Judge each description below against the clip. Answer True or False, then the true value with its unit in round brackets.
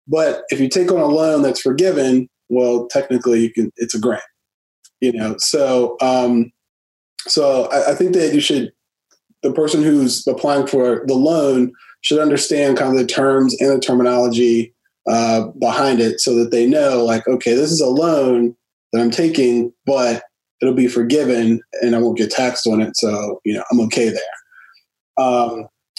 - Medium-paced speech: True (175 wpm)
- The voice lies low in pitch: True (125 Hz)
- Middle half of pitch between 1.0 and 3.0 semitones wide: True (2.6 semitones)